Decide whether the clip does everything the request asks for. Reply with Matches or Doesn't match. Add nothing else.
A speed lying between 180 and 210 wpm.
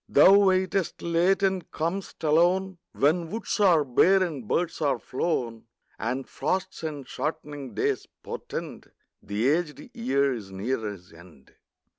Doesn't match